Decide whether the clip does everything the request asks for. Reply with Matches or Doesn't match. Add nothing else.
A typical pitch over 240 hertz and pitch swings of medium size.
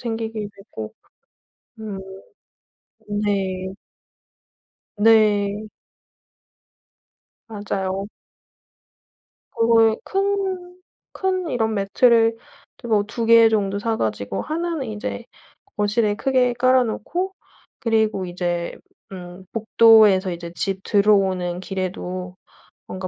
Doesn't match